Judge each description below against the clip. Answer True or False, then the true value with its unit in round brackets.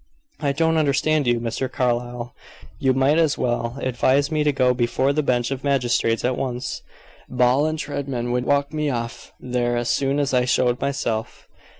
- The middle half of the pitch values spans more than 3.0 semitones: False (2.7 semitones)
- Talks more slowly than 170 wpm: False (180 wpm)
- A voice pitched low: True (130 Hz)